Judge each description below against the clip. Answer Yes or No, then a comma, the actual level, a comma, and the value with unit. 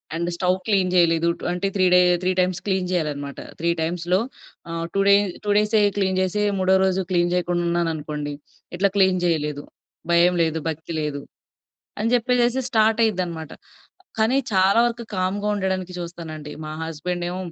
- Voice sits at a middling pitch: Yes, medium, 180 Hz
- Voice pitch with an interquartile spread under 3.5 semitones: Yes, average, 2.9 semitones